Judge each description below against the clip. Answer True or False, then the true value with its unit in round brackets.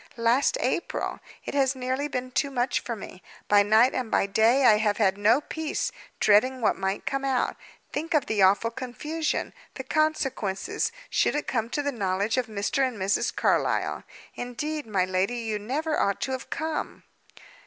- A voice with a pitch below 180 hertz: False (245 Hz)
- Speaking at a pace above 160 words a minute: True (175 wpm)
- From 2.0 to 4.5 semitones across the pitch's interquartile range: False (4.9 semitones)